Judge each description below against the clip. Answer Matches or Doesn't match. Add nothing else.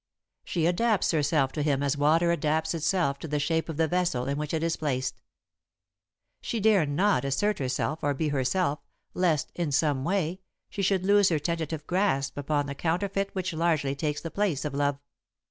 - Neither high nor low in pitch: Matches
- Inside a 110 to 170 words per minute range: Doesn't match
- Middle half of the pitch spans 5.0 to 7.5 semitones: Doesn't match